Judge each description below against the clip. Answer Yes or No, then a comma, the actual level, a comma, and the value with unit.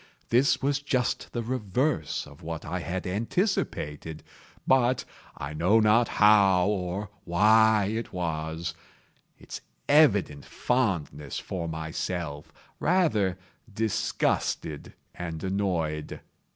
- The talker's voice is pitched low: Yes, very low, 95 Hz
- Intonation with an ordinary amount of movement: No, wide, 5.8 semitones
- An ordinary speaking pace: No, slow, 95 wpm